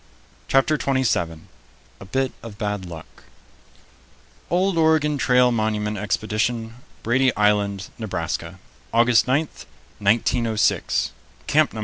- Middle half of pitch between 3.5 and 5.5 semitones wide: Yes, average, 4.2 semitones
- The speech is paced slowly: Yes, slow, 110 wpm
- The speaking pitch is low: Yes, low, 115 Hz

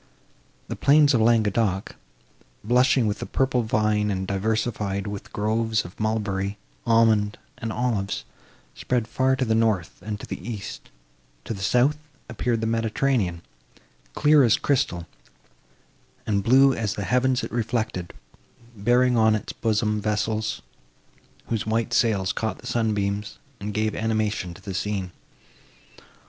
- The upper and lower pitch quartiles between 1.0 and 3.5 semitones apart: Yes, narrow, 2.5 semitones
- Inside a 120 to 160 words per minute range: Yes, slow, 135 wpm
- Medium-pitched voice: No, low, 110 Hz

